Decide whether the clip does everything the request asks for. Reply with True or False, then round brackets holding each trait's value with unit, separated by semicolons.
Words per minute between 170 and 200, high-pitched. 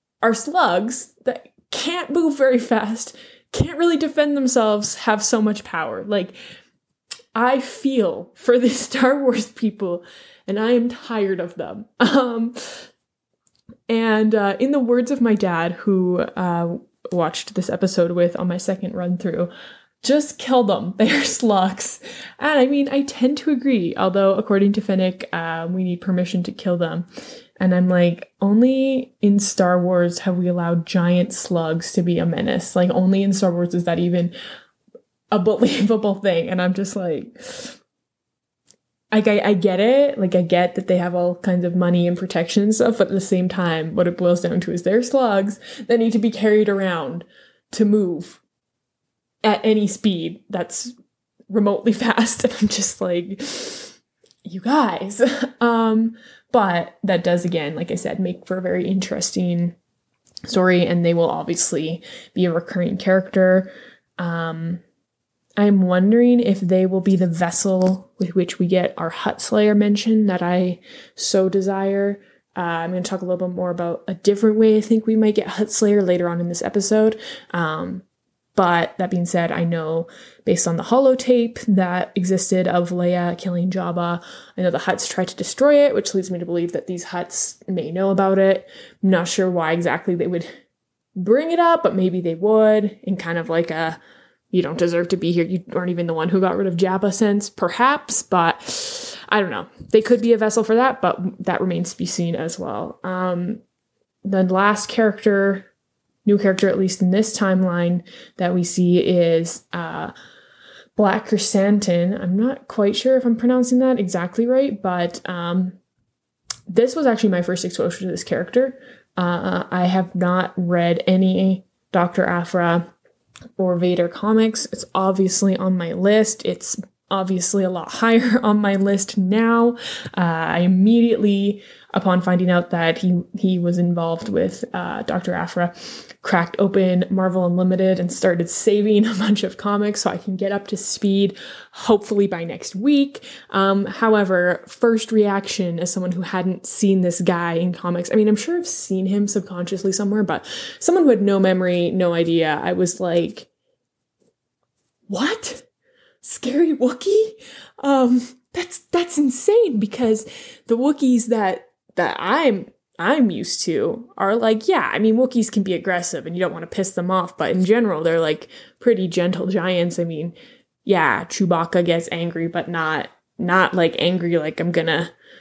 True (175 wpm; 195 Hz)